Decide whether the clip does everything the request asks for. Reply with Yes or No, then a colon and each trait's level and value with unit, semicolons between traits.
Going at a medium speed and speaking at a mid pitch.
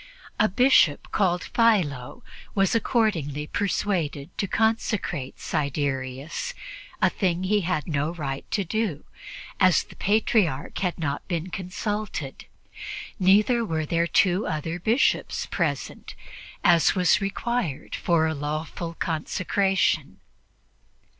No: slow, 110 wpm; medium, 175 Hz